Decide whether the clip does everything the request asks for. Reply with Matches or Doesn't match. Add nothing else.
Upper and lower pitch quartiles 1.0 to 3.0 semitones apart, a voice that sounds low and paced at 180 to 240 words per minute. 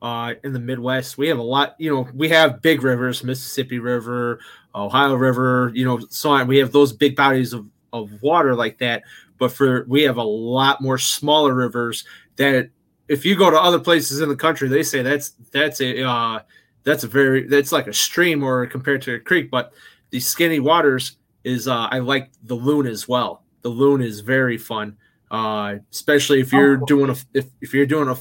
Matches